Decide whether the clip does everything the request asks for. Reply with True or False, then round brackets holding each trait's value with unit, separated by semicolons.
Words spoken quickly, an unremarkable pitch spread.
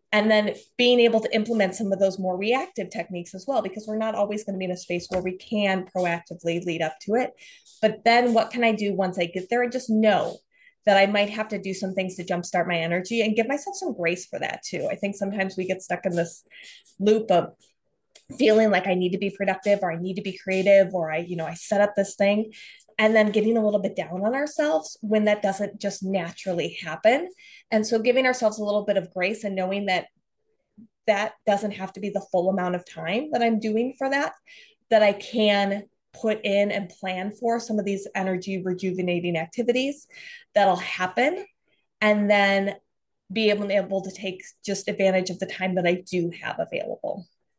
True (220 wpm; 3.0 semitones)